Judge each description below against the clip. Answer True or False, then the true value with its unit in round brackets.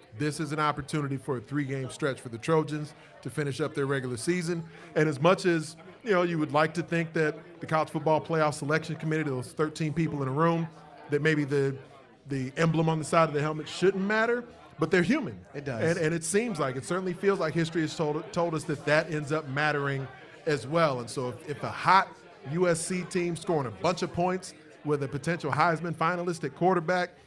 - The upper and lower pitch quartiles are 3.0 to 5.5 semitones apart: False (2.6 semitones)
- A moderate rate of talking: False (215 wpm)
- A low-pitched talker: False (155 Hz)